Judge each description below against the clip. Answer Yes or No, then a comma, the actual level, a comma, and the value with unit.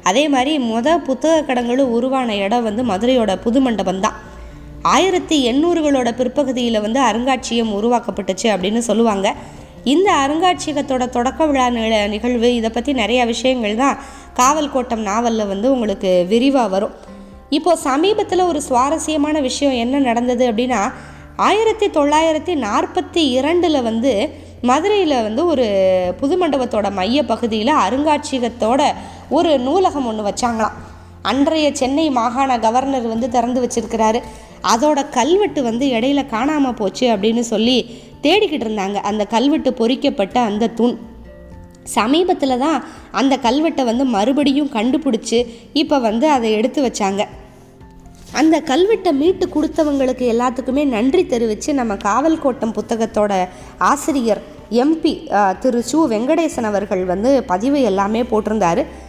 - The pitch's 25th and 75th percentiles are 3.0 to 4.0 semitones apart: No, average, 4.6 semitones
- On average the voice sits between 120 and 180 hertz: No, very high, 250 Hz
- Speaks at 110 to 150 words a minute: Yes, average, 120 wpm